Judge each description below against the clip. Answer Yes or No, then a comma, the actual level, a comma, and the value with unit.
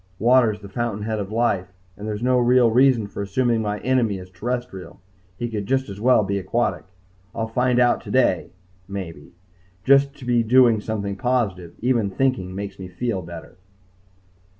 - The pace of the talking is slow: No, average, 170 wpm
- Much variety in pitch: No, average, 3.8 semitones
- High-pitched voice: No, low, 110 Hz